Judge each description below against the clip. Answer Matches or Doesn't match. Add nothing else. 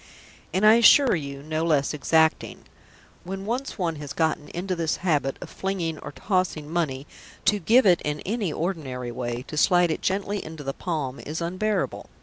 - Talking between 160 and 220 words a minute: Matches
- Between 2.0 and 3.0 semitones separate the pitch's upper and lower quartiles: Doesn't match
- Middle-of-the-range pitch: Matches